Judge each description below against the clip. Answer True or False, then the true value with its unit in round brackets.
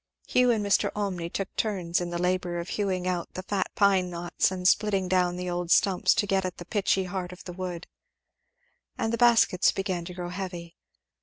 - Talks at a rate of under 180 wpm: False (205 wpm)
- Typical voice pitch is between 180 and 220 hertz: True (185 Hz)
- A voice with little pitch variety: True (1.8 semitones)